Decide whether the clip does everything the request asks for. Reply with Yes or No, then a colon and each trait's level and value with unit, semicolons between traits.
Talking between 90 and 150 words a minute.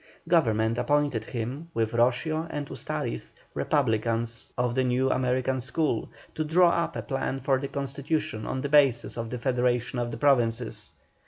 No: average, 160 wpm